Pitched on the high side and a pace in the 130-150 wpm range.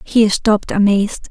Yes: high, 210 Hz; average, 140 wpm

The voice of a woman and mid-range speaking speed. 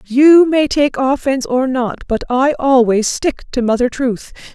Yes: female; average, 170 wpm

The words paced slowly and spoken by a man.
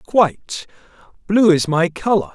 Yes: slow, 100 wpm; male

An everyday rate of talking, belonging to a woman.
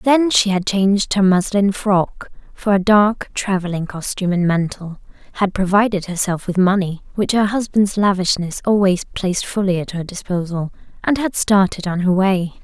Yes: average, 155 wpm; female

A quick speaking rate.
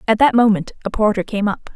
Yes: fast, 240 wpm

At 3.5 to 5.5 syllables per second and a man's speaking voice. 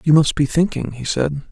Yes: 5.3 syllables/s; male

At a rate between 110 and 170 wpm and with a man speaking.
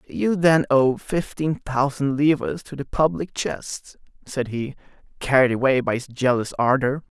Yes: average, 150 wpm; male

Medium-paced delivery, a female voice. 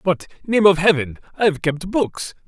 No: average, 145 wpm; male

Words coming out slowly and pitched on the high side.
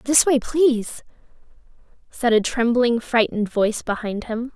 Yes: slow, 130 wpm; high, 240 Hz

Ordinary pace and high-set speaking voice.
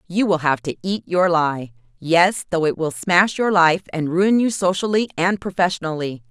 No: average, 180 wpm; medium, 175 Hz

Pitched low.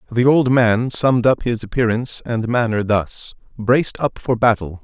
Yes: low, 115 Hz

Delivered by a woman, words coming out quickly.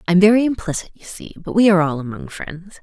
Yes: female; fast, 255 wpm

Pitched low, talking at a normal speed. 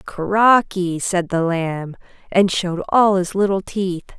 No: medium, 185 Hz; average, 145 wpm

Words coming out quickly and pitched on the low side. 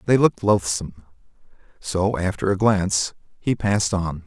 No: average, 140 wpm; very low, 95 Hz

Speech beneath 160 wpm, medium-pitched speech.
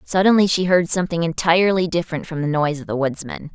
No: fast, 205 wpm; medium, 170 Hz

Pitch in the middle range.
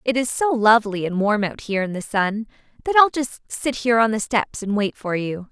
No: high, 225 Hz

